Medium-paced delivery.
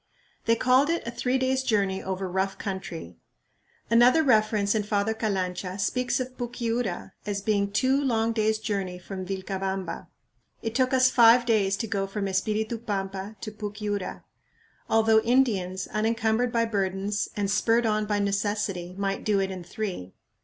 Yes: average, 155 wpm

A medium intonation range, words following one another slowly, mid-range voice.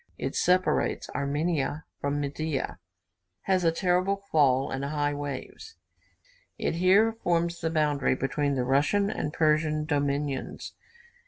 Yes: average, 3.4 semitones; slow, 120 wpm; medium, 150 Hz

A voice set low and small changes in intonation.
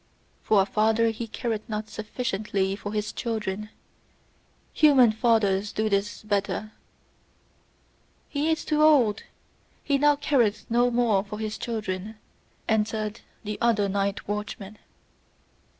No: high, 215 Hz; narrow, 2.3 semitones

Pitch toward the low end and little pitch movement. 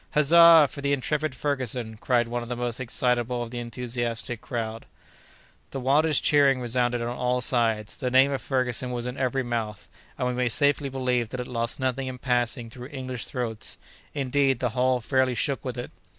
Yes: low, 125 Hz; narrow, 1.8 semitones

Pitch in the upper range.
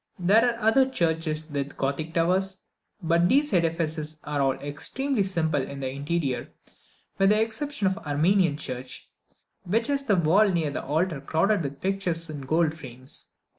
No: medium, 165 Hz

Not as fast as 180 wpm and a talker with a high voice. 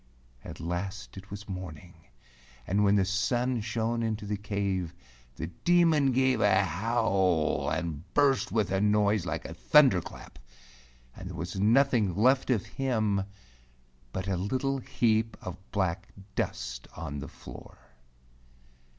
No: average, 140 wpm; low, 100 Hz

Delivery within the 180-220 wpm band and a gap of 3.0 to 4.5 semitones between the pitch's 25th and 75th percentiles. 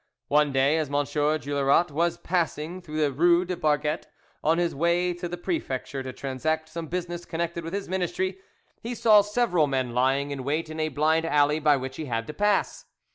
Yes: average, 195 wpm; average, 3.5 semitones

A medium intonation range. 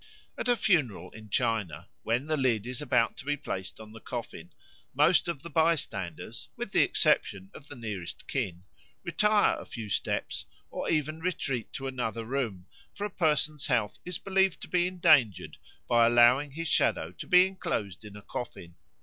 No: wide, 6.8 semitones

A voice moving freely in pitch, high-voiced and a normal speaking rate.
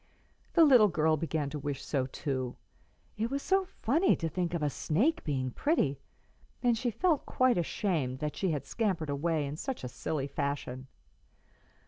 No: wide, 8.8 semitones; medium, 160 Hz; average, 170 wpm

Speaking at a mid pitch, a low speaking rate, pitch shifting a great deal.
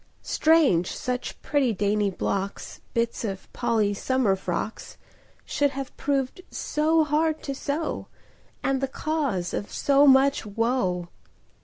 No: very high, 255 Hz; slow, 125 wpm; wide, 5.9 semitones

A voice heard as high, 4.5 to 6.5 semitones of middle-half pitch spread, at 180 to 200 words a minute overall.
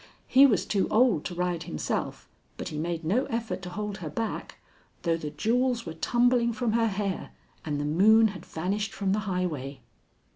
Yes: high, 195 Hz; wide, 5.4 semitones; average, 185 wpm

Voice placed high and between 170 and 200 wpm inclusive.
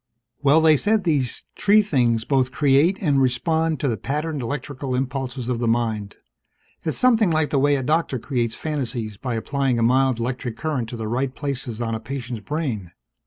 No: low, 135 Hz; average, 185 wpm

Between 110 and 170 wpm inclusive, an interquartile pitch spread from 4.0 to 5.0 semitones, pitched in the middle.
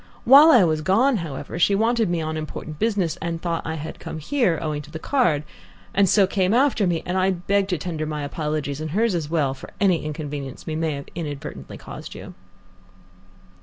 No: fast, 205 wpm; average, 4.4 semitones; medium, 165 Hz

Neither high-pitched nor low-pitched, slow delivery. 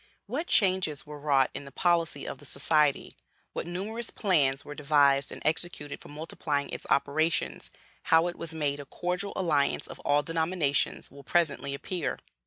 No: medium, 155 Hz; average, 165 wpm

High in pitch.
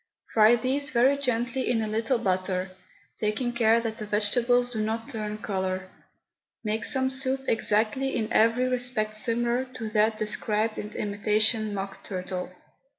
Yes: high, 220 Hz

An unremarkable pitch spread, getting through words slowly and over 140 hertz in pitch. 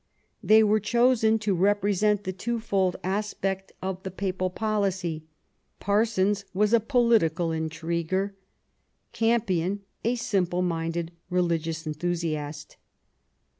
Yes: average, 3.8 semitones; slow, 120 wpm; high, 190 Hz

